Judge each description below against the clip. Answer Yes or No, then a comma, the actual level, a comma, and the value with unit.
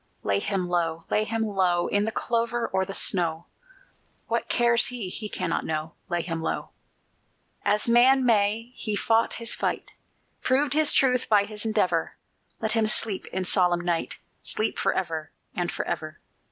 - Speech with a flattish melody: No, average, 4.8 semitones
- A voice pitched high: Yes, high, 205 Hz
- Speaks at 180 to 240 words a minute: No, average, 160 wpm